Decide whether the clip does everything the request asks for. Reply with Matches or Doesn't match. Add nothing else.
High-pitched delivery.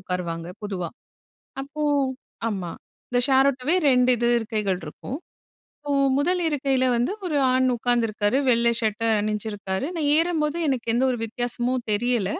Matches